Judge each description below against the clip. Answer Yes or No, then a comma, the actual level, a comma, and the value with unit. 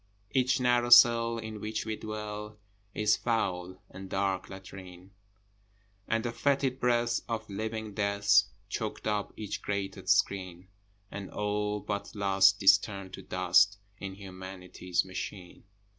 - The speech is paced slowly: Yes, slow, 130 wpm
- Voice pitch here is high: No, low, 105 Hz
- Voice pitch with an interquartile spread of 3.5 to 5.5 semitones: No, narrow, 2.4 semitones